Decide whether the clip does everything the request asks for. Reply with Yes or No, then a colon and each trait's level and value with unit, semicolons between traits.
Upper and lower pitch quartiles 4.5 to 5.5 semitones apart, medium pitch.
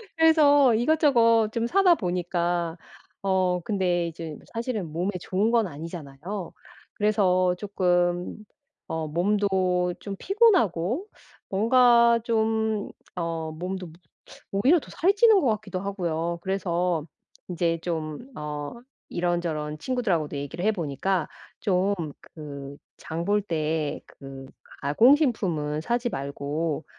Yes: average, 5.2 semitones; medium, 180 Hz